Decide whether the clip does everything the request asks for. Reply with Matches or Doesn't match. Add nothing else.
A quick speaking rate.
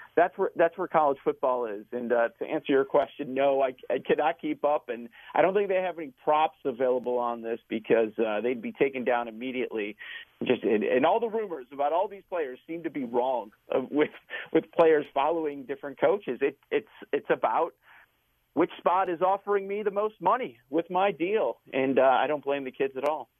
Matches